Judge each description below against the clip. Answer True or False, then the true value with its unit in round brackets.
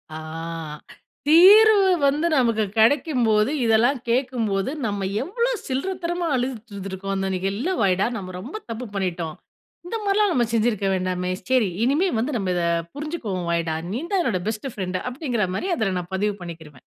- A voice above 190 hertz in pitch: True (225 Hz)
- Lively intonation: True (7.1 semitones)